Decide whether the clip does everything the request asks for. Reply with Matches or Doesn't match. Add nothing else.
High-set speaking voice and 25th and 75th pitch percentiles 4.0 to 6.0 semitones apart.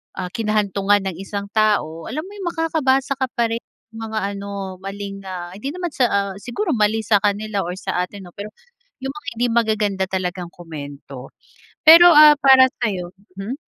Matches